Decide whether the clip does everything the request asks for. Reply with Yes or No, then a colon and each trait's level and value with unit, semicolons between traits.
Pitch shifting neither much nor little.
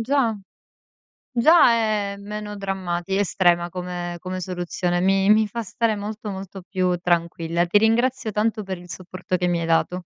Yes: average, 3.3 semitones